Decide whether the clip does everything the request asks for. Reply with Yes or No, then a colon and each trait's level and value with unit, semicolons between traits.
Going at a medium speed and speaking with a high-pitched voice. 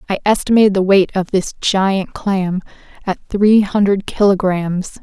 Yes: average, 145 wpm; high, 195 Hz